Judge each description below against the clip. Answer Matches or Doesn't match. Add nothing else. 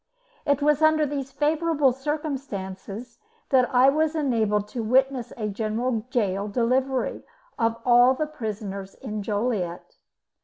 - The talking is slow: Matches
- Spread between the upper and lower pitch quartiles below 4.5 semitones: Doesn't match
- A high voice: Matches